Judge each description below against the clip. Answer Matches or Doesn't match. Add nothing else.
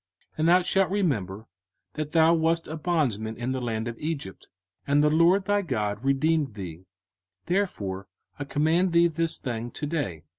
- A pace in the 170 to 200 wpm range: Matches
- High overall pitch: Doesn't match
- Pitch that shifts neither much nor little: Doesn't match